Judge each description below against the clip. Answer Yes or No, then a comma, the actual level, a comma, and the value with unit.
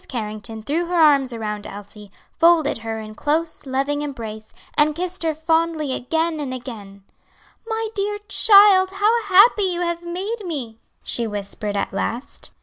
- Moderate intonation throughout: No, wide, 7.7 semitones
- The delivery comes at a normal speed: Yes, average, 150 wpm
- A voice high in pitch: Yes, very high, 295 Hz